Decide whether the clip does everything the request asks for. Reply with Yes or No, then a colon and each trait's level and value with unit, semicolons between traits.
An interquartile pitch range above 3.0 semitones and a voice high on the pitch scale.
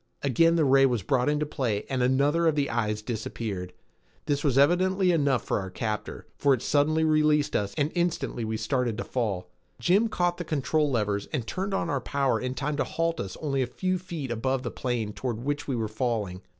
No: average, 5.1 semitones; low, 135 Hz